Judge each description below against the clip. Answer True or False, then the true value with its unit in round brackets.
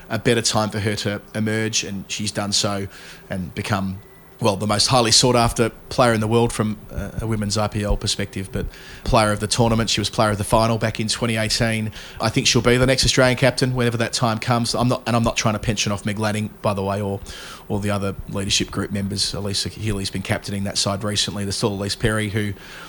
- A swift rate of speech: True (230 wpm)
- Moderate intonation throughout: False (2.2 semitones)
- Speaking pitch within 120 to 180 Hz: False (105 Hz)